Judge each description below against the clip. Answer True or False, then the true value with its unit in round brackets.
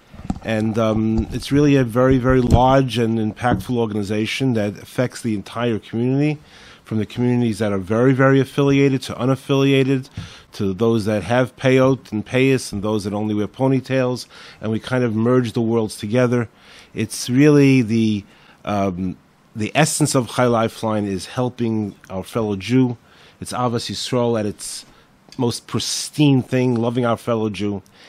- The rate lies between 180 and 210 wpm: False (165 wpm)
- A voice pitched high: False (120 Hz)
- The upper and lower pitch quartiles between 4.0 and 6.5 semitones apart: False (3.3 semitones)